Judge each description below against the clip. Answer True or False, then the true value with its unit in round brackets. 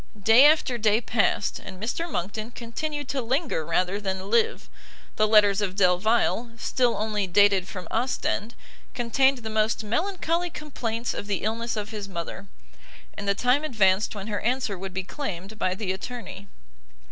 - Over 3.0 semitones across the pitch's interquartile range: True (3.8 semitones)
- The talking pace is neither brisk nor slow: True (160 wpm)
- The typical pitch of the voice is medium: False (215 Hz)